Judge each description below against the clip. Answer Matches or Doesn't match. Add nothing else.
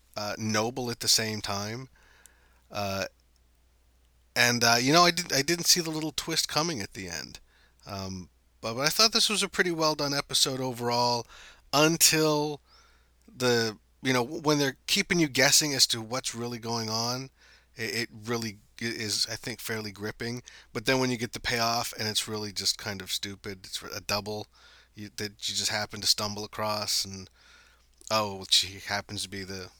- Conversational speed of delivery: Matches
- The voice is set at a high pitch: Doesn't match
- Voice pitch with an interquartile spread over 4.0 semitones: Matches